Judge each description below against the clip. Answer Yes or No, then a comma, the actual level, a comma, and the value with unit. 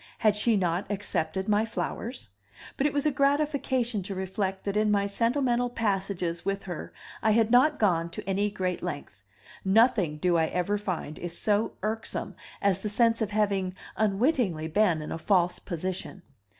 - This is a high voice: Yes, high, 200 Hz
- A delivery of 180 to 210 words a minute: No, average, 170 wpm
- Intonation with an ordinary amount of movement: Yes, average, 3.8 semitones